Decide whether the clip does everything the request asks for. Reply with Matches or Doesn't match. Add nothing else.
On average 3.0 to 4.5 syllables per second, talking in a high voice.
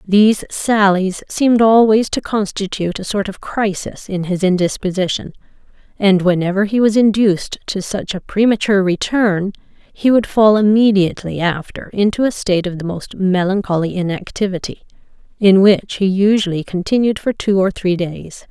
Doesn't match